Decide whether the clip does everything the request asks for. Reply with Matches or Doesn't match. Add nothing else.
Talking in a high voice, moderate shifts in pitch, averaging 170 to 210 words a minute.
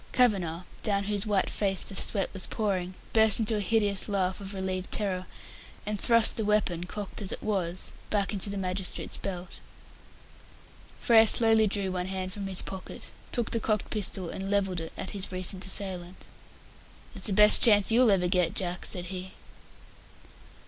Doesn't match